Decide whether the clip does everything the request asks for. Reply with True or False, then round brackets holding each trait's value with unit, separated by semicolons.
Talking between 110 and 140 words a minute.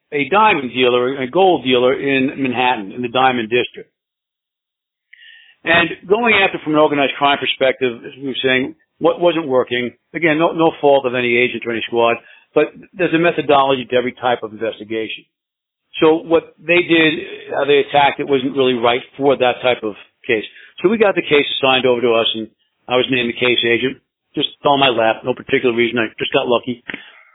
False (195 wpm)